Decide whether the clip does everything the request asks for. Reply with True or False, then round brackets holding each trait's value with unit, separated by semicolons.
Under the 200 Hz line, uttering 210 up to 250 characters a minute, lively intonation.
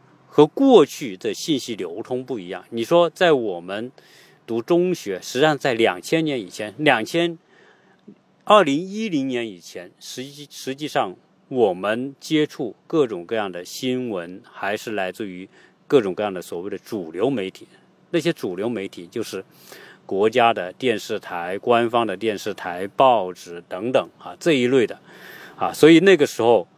True (135 Hz; 240 characters per minute; 6.8 semitones)